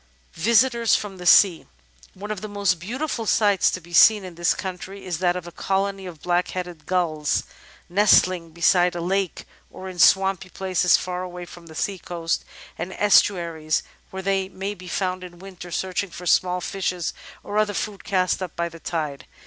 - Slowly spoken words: No, average, 180 wpm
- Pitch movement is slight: Yes, narrow, 2.0 semitones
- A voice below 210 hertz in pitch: Yes, medium, 185 Hz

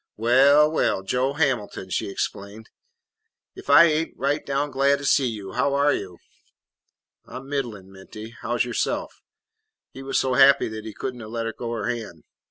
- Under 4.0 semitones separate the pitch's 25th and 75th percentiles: No, average, 4.4 semitones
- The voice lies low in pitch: Yes, low, 125 Hz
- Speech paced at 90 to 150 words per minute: No, average, 175 wpm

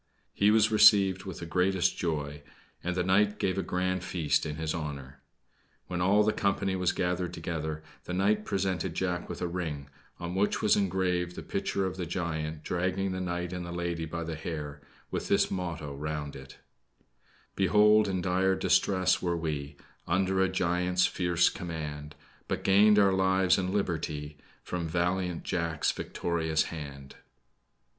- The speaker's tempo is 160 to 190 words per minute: Yes, average, 165 wpm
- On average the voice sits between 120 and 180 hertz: No, very low, 90 Hz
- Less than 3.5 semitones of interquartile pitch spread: Yes, average, 2.9 semitones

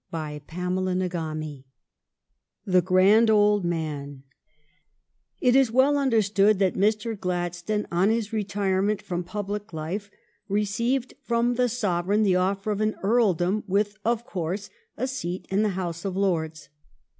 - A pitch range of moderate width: Yes, average, 3.4 semitones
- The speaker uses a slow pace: No, average, 145 wpm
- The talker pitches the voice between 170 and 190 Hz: No, high, 200 Hz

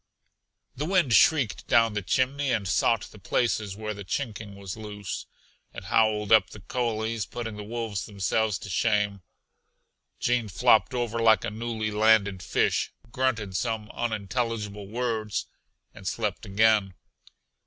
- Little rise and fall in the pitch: Yes, narrow, 2.2 semitones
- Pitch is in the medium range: No, low, 110 Hz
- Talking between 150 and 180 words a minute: No, average, 140 wpm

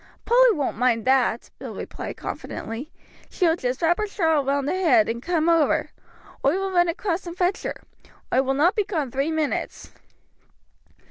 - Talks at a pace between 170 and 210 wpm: Yes, average, 180 wpm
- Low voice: No, very high, 320 Hz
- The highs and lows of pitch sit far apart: No, average, 4.9 semitones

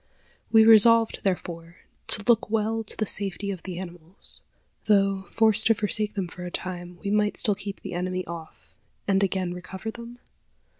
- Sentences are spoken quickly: No, average, 170 wpm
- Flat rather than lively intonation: No, average, 3.2 semitones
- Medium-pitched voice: No, high, 195 Hz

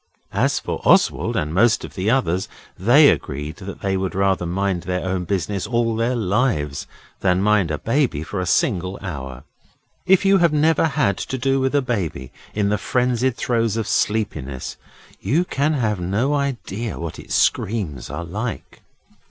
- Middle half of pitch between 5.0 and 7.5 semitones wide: Yes, wide, 5.6 semitones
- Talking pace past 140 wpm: Yes, average, 170 wpm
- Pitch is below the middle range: Yes, low, 105 Hz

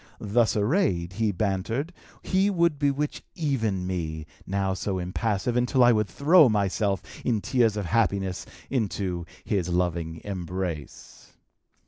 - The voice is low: Yes, low, 100 Hz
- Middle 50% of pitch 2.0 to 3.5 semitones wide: No, average, 5.1 semitones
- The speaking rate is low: Yes, slow, 125 wpm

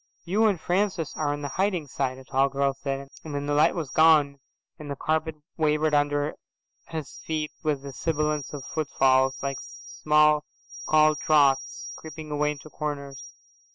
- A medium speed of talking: Yes, average, 165 wpm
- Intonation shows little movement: Yes, narrow, 2.0 semitones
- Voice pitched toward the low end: No, medium, 150 Hz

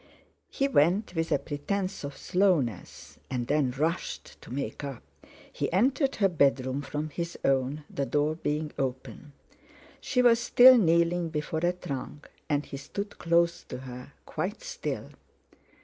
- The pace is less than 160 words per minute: Yes, average, 150 wpm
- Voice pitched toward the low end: No, medium, 155 Hz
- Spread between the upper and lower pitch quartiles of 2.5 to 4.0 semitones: No, average, 4.5 semitones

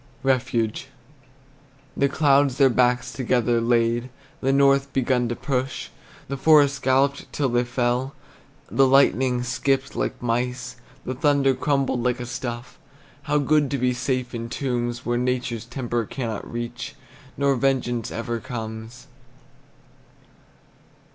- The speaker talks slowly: Yes, slow, 130 wpm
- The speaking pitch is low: Yes, low, 125 Hz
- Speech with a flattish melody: Yes, narrow, 2.2 semitones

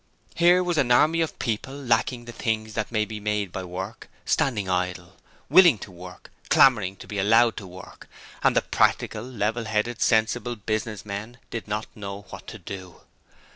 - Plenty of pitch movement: No, average, 3.3 semitones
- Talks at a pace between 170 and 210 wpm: Yes, average, 175 wpm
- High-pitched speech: No, low, 110 Hz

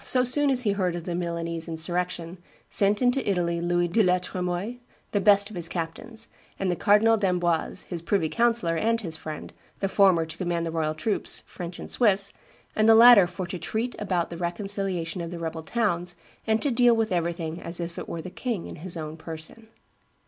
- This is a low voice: No, medium, 180 Hz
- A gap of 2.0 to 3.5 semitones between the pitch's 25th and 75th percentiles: No, average, 4.1 semitones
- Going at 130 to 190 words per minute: No, fast, 205 wpm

